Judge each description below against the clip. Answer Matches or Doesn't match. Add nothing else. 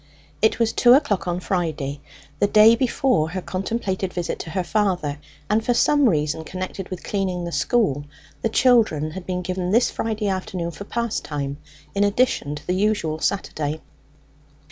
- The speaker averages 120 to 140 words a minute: Doesn't match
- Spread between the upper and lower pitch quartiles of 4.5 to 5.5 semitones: Matches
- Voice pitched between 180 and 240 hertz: Matches